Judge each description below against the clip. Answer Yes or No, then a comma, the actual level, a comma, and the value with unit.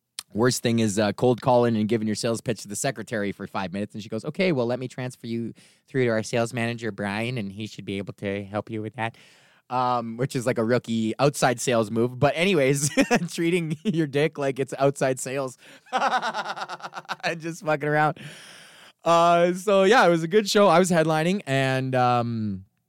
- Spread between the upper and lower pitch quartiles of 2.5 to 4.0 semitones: No, wide, 5.4 semitones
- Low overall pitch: Yes, low, 125 Hz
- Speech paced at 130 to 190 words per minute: No, average, 200 wpm